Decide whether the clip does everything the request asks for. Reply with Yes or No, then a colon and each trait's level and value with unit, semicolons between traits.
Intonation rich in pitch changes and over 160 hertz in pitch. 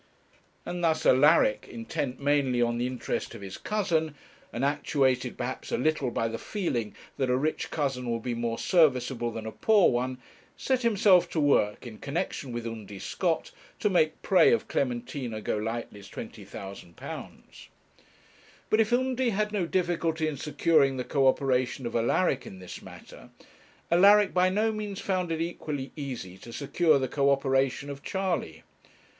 No: wide, 6.3 semitones; medium, 140 Hz